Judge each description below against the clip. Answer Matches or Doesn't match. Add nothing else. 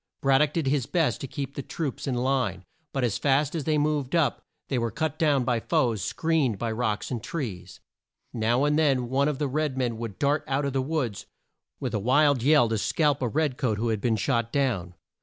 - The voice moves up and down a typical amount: Matches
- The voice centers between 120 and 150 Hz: Matches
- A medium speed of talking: Doesn't match